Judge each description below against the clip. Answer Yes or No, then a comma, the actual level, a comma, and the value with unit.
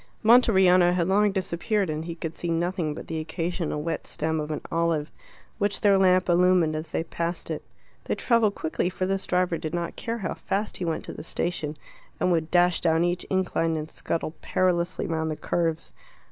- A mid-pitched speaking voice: Yes, medium, 175 Hz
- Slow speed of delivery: No, average, 195 wpm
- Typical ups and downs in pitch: No, narrow, 2.3 semitones